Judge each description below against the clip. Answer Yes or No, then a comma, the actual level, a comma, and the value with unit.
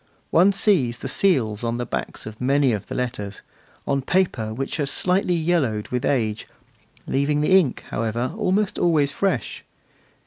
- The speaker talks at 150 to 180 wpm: Yes, average, 165 wpm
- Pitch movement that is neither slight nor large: No, wide, 6.9 semitones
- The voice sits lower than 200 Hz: Yes, medium, 140 Hz